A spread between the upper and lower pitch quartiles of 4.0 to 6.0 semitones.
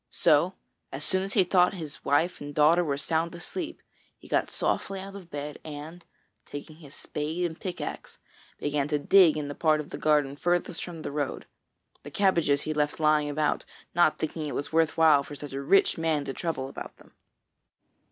No: average, 3.0 semitones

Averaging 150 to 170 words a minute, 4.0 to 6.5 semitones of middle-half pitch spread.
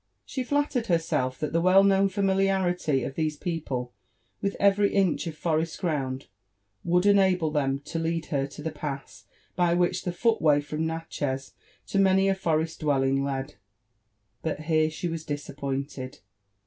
Yes: average, 160 wpm; average, 4.7 semitones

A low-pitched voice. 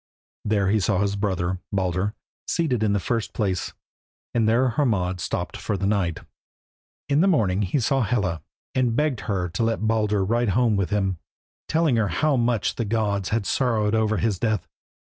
Yes: low, 105 Hz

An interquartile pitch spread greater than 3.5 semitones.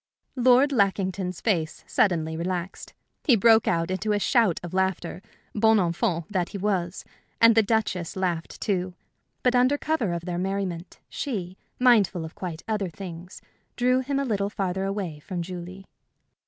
Yes: average, 4.0 semitones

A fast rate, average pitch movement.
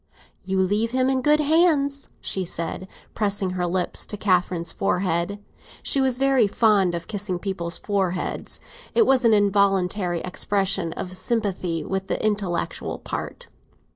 No: average, 140 wpm; average, 4.2 semitones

